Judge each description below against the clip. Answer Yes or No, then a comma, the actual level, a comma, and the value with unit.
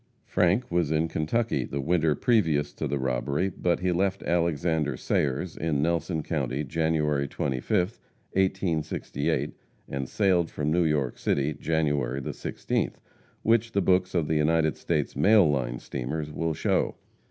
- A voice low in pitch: Yes, very low, 80 Hz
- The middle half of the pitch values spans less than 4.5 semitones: Yes, average, 3.6 semitones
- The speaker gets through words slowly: No, average, 150 wpm